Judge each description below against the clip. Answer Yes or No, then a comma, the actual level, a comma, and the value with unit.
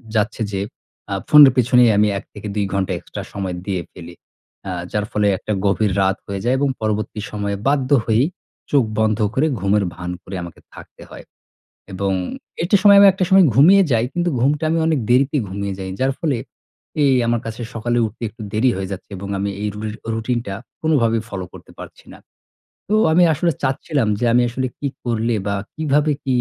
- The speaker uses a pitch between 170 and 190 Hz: No, low, 115 Hz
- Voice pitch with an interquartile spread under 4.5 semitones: No, wide, 5.6 semitones